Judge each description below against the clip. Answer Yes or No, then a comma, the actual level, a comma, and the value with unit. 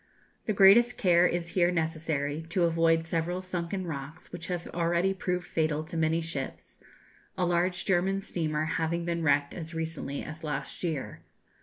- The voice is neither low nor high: Yes, medium, 170 Hz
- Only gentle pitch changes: Yes, narrow, 1.9 semitones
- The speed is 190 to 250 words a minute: No, average, 160 wpm